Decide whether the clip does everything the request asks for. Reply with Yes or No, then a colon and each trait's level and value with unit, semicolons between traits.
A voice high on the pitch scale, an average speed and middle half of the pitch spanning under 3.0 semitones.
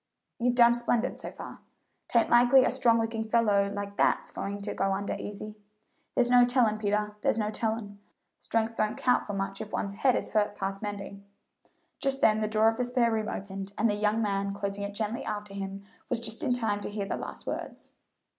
No: high, 215 Hz; fast, 210 wpm; narrow, 2.4 semitones